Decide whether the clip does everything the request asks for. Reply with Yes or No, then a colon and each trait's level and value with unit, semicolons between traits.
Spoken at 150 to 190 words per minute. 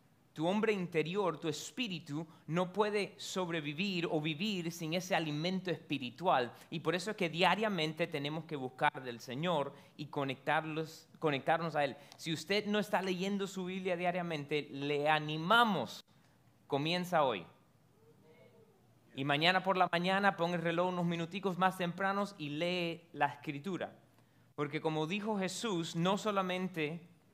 No: average, 140 wpm